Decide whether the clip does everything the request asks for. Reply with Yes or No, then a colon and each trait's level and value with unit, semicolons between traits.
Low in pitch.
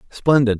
Yes: low, 125 Hz